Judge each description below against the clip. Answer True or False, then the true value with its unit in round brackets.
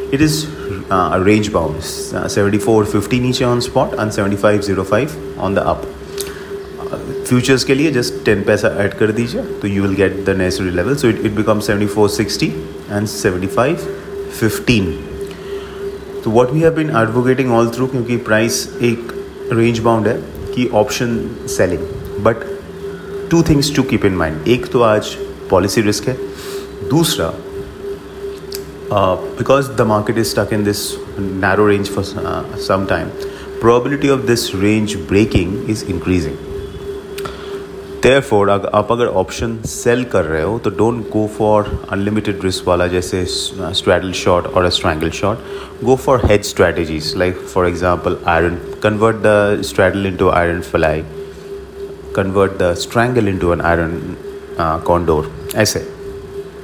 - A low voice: True (110 Hz)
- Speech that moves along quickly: False (145 wpm)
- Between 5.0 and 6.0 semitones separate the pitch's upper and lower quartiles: True (5.5 semitones)